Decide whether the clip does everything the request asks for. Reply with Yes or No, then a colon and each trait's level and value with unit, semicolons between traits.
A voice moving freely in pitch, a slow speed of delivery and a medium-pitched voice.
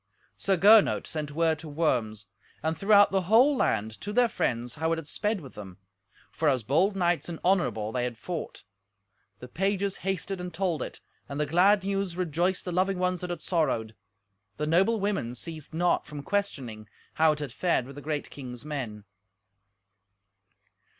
No: wide, 5.7 semitones; average, 175 wpm; medium, 165 Hz